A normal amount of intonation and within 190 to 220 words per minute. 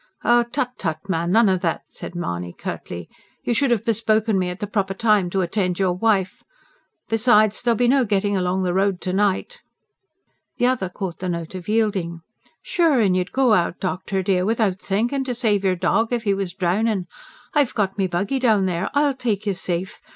Yes: average, 3.8 semitones; average, 195 wpm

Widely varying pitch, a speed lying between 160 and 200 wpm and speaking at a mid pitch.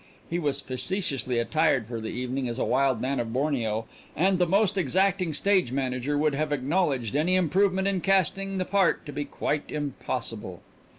Yes: wide, 6.4 semitones; average, 175 wpm; medium, 145 Hz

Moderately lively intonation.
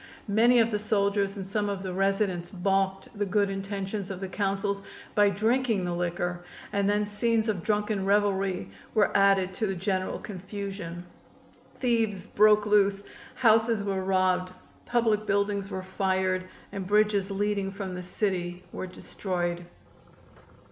No: narrow, 1.8 semitones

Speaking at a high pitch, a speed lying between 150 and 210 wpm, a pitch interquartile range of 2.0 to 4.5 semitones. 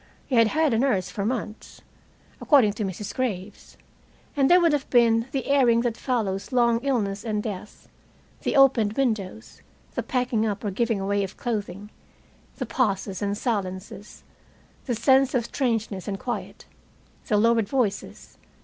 Yes: high, 225 Hz; average, 155 wpm; average, 3.7 semitones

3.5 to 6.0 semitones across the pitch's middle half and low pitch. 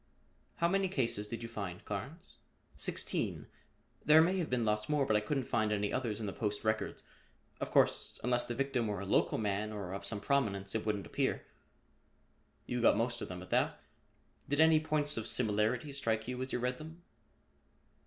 Yes: average, 4.7 semitones; low, 115 Hz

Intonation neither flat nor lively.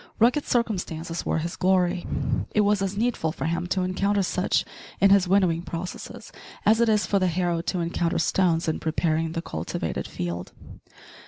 Yes: average, 3.1 semitones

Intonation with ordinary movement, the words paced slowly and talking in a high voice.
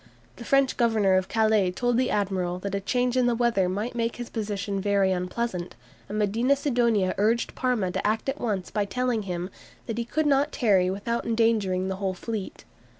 No: average, 3.8 semitones; average, 195 wpm; high, 215 Hz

